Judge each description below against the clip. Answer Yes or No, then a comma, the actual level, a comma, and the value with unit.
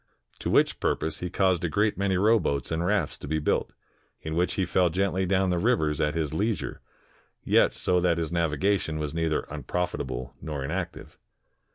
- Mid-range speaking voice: No, very low, 85 Hz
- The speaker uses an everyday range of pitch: Yes, average, 3.5 semitones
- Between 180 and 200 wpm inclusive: Yes, average, 185 wpm